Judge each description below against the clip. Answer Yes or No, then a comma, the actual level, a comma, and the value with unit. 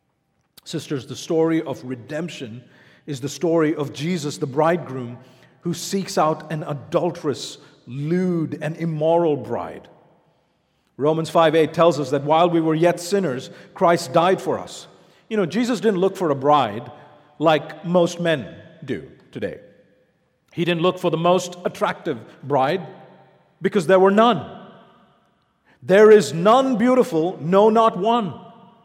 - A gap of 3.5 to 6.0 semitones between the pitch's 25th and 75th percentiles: Yes, average, 3.8 semitones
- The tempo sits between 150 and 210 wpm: No, average, 140 wpm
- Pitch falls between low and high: Yes, medium, 165 Hz